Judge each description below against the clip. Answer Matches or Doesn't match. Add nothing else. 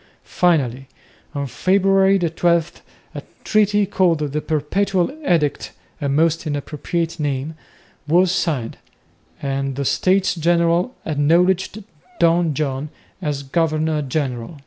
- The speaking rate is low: Matches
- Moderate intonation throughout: Matches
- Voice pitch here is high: Doesn't match